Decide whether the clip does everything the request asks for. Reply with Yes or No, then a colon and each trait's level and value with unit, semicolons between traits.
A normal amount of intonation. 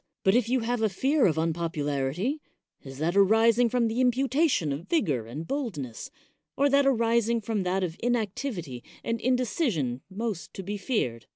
No: wide, 7.2 semitones